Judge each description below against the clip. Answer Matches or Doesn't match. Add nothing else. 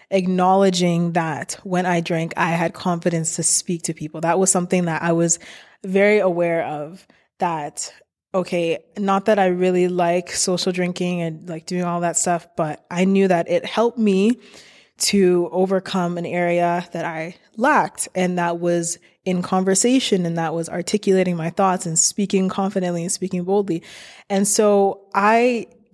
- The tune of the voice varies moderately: Doesn't match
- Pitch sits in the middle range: Matches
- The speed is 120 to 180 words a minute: Matches